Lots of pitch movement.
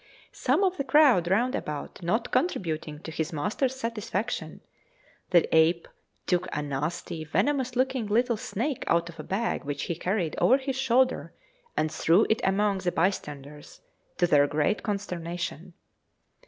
Yes: wide, 7.3 semitones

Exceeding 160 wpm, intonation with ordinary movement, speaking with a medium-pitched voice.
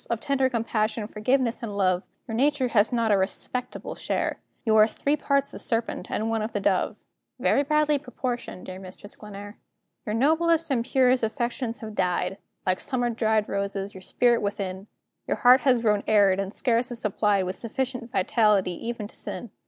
No: average, 180 wpm; average, 3.6 semitones; high, 225 Hz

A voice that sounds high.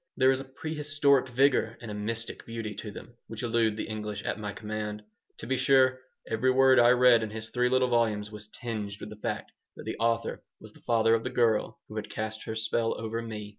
No: low, 115 Hz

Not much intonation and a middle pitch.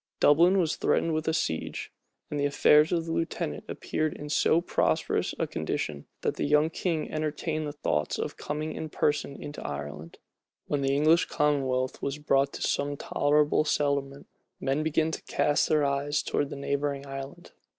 Yes: narrow, 2.0 semitones; medium, 145 Hz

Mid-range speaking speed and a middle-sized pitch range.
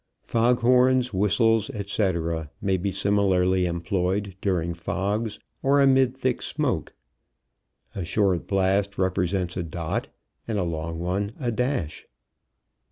No: slow, 120 wpm; average, 4.0 semitones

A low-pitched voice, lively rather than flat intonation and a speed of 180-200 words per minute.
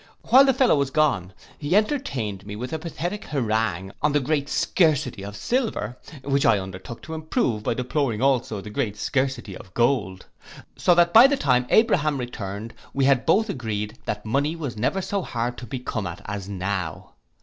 Yes: low, 125 Hz; wide, 6.7 semitones; average, 185 wpm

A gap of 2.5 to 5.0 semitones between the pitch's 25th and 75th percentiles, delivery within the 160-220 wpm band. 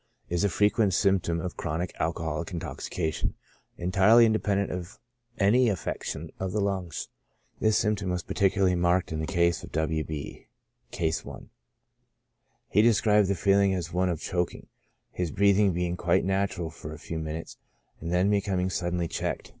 Yes: average, 2.9 semitones; average, 165 wpm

